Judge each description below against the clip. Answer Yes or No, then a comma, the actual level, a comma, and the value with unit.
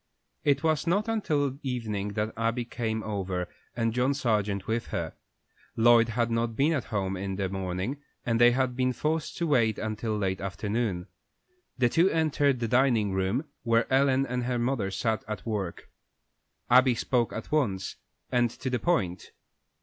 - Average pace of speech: Yes, average, 165 wpm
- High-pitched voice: No, low, 115 Hz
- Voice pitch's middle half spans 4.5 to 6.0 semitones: No, average, 3.9 semitones